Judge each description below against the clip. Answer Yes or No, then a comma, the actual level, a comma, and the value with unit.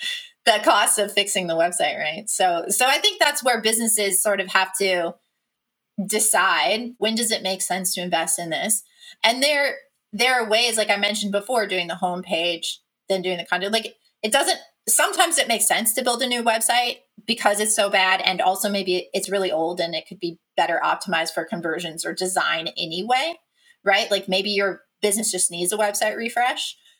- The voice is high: Yes, high, 205 Hz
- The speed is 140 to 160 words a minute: No, average, 195 wpm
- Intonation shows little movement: No, average, 4.1 semitones